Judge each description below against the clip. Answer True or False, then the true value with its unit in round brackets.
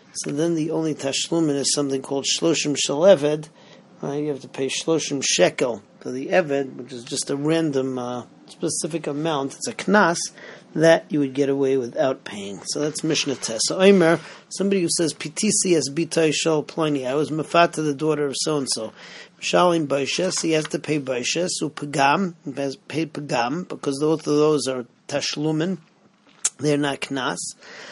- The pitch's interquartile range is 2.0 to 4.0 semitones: True (2.9 semitones)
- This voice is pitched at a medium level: True (150 Hz)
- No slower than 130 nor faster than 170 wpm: True (165 wpm)